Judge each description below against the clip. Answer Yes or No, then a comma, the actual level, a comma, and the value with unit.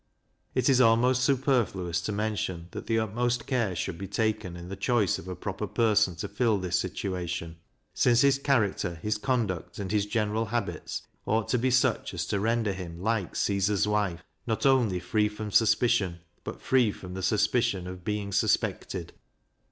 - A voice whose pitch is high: No, low, 105 Hz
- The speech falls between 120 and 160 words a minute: No, average, 175 wpm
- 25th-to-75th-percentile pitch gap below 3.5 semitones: No, average, 3.9 semitones